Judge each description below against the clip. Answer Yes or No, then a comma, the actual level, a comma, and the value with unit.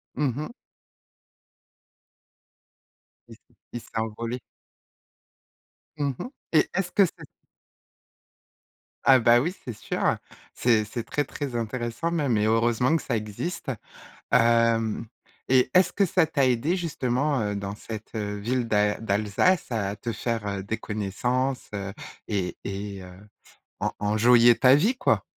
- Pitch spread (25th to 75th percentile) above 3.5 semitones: Yes, average, 4.1 semitones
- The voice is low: Yes, low, 115 Hz